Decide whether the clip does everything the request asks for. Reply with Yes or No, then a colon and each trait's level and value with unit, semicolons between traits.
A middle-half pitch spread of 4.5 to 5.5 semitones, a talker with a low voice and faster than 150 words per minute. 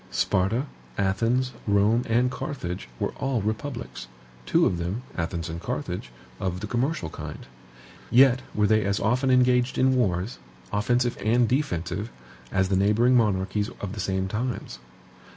No: average, 4.8 semitones; low, 105 Hz; average, 145 wpm